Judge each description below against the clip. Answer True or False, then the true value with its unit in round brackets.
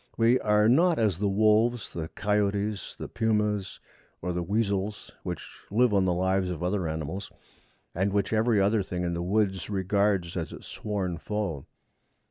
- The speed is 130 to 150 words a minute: False (165 wpm)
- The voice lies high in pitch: False (100 Hz)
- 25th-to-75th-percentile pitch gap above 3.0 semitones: False (2.7 semitones)